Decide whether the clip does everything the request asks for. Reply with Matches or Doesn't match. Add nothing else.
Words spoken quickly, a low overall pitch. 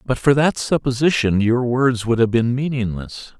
Doesn't match